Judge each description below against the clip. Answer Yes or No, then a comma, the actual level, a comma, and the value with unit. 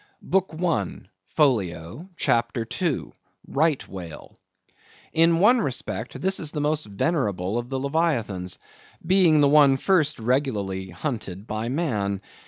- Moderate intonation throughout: No, wide, 8.0 semitones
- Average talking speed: No, slow, 120 wpm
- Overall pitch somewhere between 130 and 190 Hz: Yes, low, 135 Hz